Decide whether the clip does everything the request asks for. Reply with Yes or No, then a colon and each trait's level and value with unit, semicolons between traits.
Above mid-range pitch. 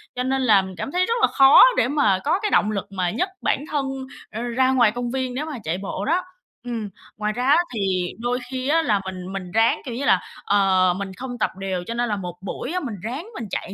Yes: high, 240 Hz